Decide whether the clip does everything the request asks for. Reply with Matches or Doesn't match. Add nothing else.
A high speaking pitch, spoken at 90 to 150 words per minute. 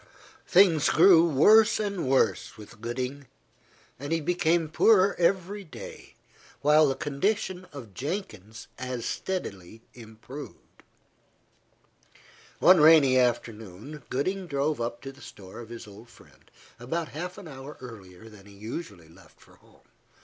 Doesn't match